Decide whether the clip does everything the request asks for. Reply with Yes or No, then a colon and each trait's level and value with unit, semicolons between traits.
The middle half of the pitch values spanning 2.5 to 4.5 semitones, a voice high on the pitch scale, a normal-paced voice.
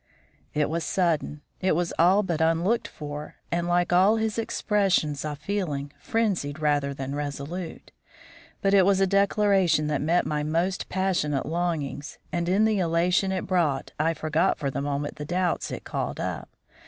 No: average, 4.2 semitones; medium, 170 Hz; average, 165 wpm